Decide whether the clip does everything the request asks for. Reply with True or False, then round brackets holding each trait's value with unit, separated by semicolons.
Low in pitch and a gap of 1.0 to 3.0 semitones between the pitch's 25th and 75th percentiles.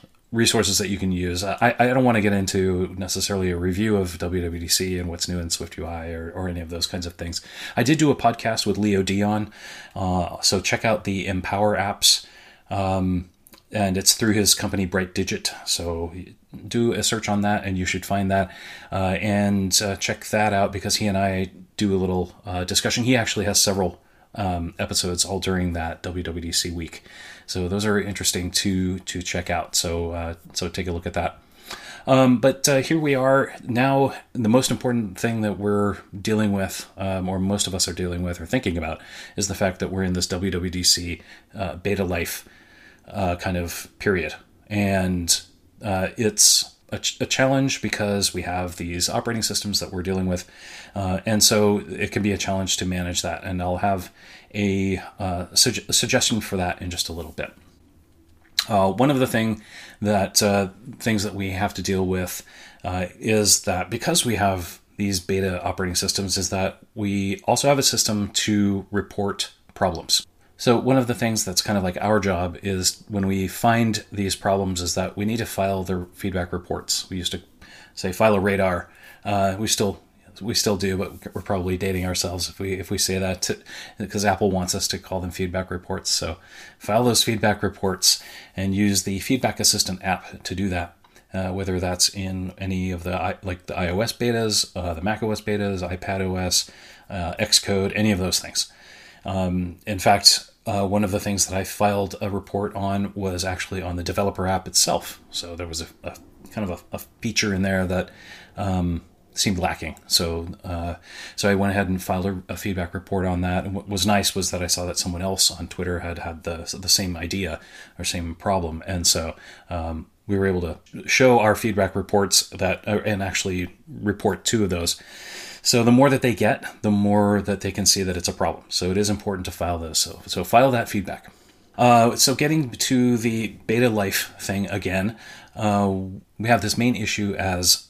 True (95 Hz; 2.4 semitones)